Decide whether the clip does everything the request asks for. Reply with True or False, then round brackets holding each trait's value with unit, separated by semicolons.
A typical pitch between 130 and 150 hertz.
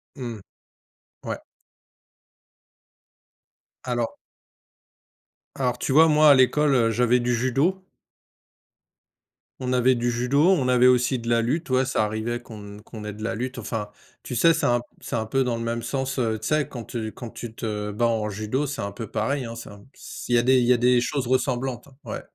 False (120 Hz)